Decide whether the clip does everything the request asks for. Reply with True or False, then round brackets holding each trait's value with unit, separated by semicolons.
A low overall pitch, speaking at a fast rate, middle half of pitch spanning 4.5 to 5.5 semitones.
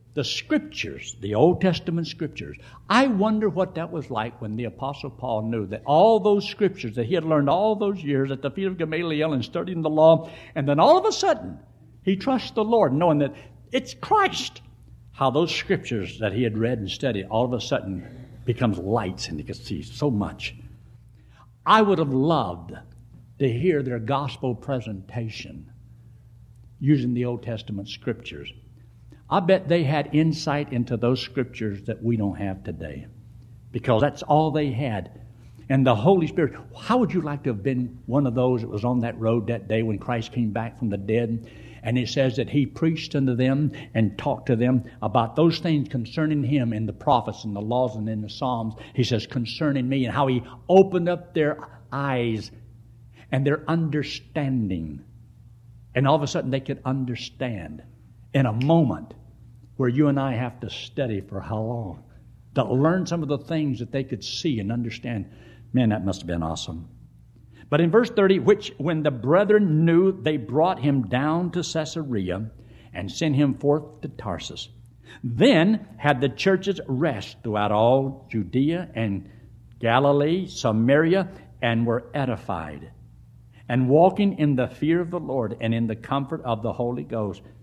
False (125 Hz; 180 wpm; 4.8 semitones)